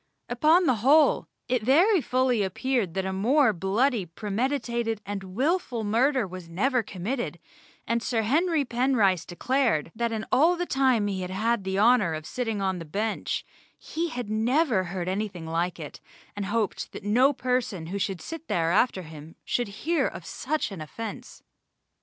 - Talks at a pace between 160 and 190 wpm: Yes, average, 165 wpm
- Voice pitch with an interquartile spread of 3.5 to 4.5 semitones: No, average, 5.3 semitones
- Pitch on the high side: Yes, high, 225 Hz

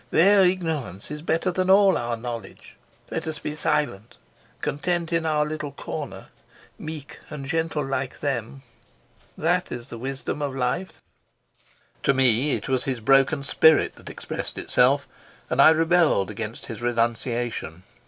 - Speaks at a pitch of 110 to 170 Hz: Yes, medium, 140 Hz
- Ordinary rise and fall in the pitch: Yes, average, 4.9 semitones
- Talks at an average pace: Yes, average, 145 wpm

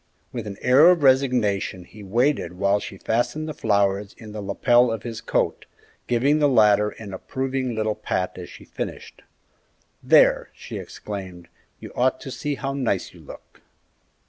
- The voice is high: No, low, 115 Hz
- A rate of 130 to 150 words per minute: No, average, 165 wpm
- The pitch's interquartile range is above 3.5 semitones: Yes, average, 4.7 semitones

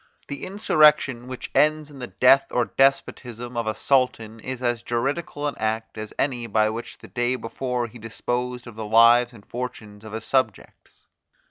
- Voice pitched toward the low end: Yes, low, 120 Hz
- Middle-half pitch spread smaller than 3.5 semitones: Yes, average, 2.9 semitones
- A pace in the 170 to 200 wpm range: Yes, average, 175 wpm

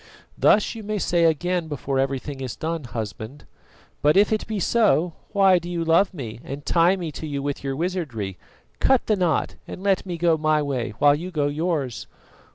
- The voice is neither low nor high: Yes, medium, 160 Hz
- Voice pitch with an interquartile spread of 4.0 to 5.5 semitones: Yes, average, 4.6 semitones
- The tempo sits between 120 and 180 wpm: No, average, 195 wpm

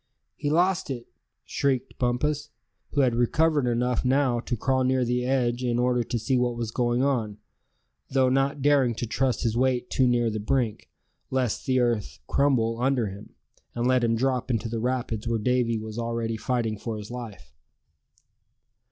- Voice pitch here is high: No, low, 125 Hz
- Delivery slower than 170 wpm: No, average, 175 wpm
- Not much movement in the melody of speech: Yes, narrow, 2.1 semitones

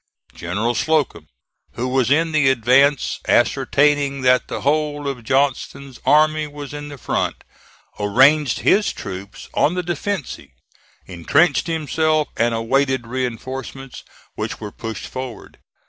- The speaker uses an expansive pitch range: No, average, 3.7 semitones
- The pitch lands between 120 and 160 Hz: Yes, low, 135 Hz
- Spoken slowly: Yes, slow, 125 wpm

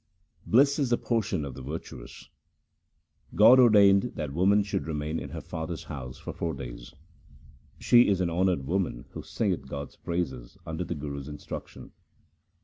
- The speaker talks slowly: No, average, 165 wpm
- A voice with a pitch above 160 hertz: No, very low, 85 Hz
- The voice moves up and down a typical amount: No, wide, 6.1 semitones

